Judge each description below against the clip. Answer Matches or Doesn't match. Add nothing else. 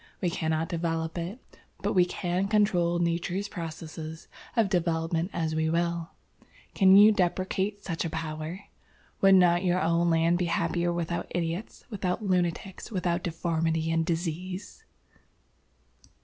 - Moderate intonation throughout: Doesn't match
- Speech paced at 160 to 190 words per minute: Doesn't match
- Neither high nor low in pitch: Matches